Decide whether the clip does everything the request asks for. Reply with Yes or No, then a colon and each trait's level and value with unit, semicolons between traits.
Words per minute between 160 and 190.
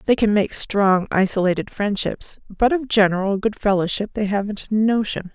Yes: average, 170 wpm